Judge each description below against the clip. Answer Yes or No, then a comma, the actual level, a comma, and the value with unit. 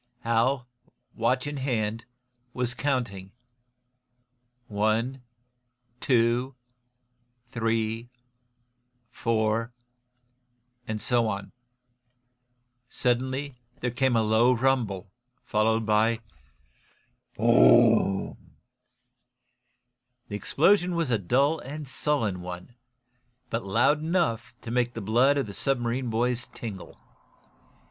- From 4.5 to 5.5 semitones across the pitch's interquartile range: No, average, 2.7 semitones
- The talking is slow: Yes, slow, 95 wpm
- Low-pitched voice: Yes, low, 120 Hz